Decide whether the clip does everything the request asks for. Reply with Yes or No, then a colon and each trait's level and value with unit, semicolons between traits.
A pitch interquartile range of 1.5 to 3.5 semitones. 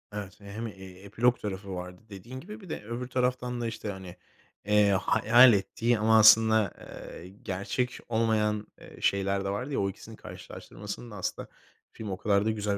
Yes: average, 3.0 semitones